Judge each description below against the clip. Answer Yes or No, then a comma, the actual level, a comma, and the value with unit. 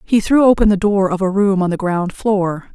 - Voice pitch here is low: No, high, 195 Hz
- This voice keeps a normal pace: No, fast, 260 wpm